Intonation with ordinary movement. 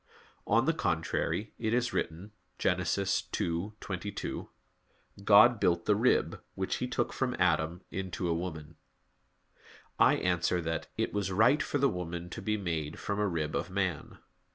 Yes: average, 4.0 semitones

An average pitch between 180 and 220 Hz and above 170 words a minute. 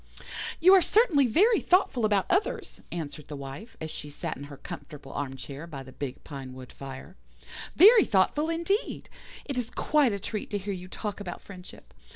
Yes: high, 190 Hz; average, 180 wpm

